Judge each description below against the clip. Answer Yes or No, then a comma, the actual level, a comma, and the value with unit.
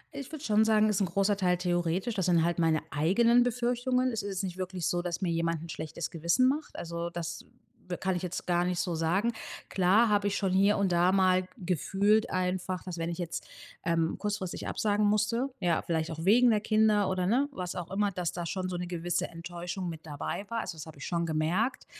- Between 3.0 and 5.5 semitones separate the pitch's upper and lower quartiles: Yes, average, 3.5 semitones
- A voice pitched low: No, medium, 185 Hz